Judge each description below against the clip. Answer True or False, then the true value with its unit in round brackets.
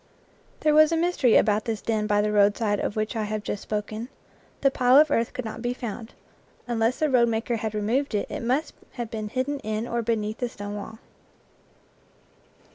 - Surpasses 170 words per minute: True (200 wpm)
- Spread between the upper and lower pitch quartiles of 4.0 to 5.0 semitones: False (2.8 semitones)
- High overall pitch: True (225 Hz)